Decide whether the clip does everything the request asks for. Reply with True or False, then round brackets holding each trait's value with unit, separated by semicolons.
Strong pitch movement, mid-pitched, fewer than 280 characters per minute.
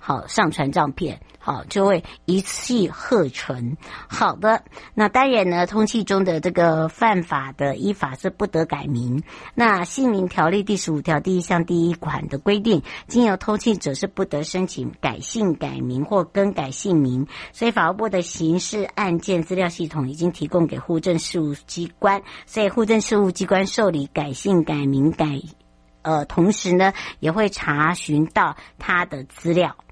False (4.6 semitones; 175 Hz; 250 characters per minute)